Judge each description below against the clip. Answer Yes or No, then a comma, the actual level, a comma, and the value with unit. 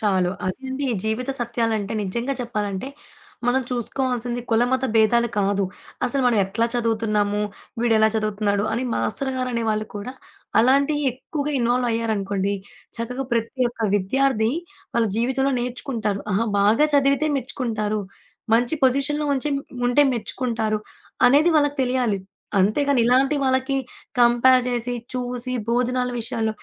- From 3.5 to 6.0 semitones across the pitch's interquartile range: No, average, 3.1 semitones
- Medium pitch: No, high, 240 Hz